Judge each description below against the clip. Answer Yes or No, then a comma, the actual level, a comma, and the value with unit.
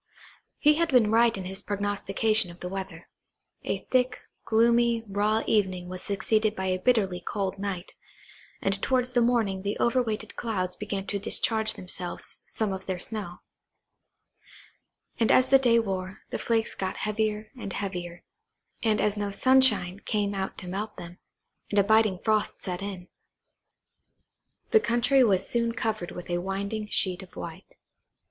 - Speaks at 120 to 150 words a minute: No, average, 160 wpm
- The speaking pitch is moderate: No, high, 205 Hz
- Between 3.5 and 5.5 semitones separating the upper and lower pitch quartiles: No, average, 3.0 semitones